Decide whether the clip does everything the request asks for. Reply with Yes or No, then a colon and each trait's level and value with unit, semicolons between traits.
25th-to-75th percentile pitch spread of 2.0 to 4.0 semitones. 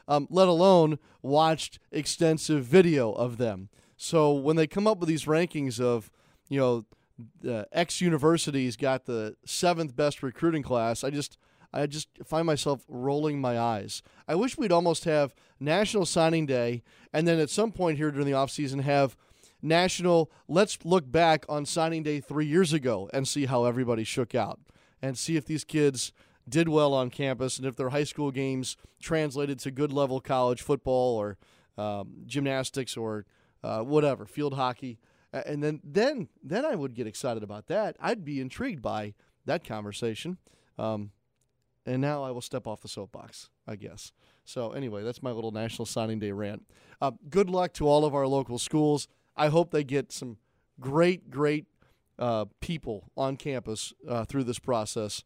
No: average, 4.5 semitones